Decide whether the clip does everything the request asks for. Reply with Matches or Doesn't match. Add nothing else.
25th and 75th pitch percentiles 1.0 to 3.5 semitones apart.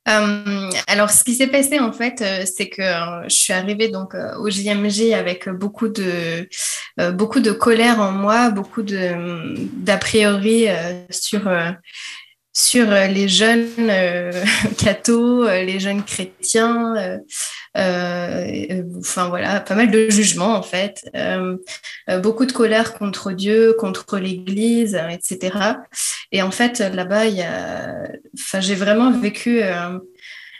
Matches